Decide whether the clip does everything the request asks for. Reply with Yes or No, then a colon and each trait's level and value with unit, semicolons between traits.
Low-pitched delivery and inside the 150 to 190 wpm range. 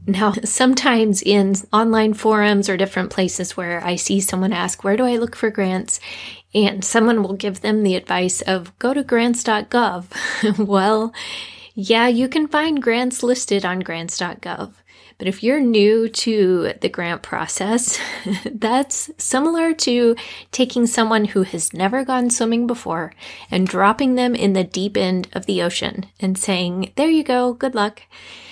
No: high, 215 Hz; average, 160 wpm